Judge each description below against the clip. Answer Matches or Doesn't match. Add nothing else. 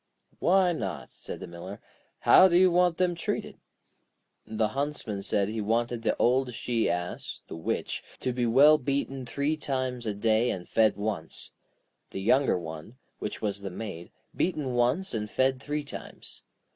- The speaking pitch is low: Matches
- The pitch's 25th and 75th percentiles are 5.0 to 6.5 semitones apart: Matches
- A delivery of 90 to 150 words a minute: Doesn't match